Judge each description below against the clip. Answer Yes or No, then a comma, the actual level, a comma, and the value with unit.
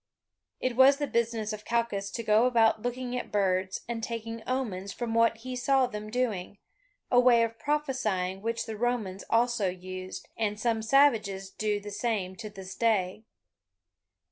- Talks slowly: No, average, 165 wpm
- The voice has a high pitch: Yes, high, 225 Hz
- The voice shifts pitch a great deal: No, average, 3.3 semitones